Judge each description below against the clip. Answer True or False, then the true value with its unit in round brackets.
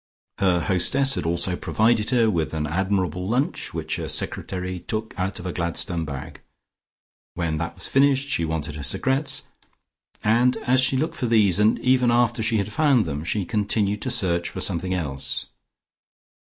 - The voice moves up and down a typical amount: False (5.9 semitones)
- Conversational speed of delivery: True (170 wpm)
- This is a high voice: False (100 Hz)